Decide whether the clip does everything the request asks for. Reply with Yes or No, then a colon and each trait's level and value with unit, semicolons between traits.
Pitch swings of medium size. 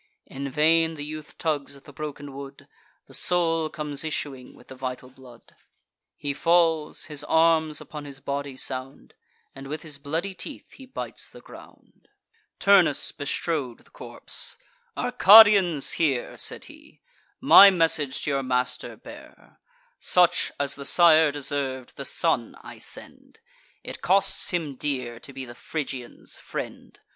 Yes: average, 3.2 semitones